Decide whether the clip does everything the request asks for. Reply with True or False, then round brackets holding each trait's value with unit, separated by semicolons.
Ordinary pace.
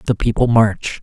True (175 wpm)